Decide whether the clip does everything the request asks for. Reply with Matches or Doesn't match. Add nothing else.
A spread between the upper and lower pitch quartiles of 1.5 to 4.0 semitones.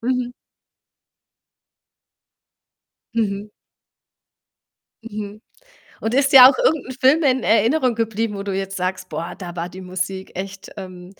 Doesn't match